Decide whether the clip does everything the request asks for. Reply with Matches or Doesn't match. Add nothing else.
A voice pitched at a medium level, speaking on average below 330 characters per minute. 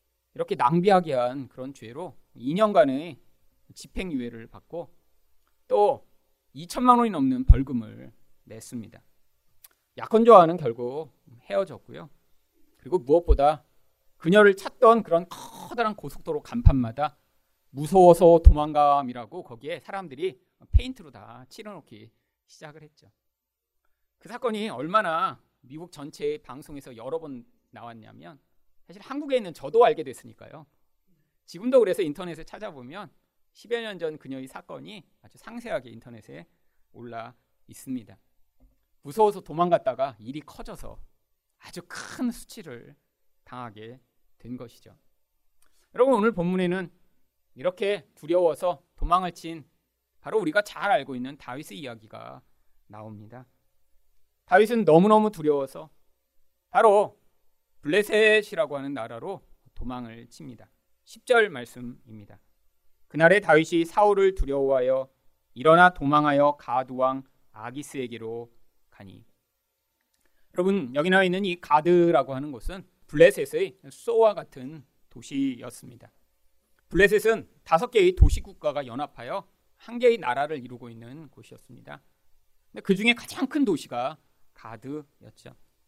Matches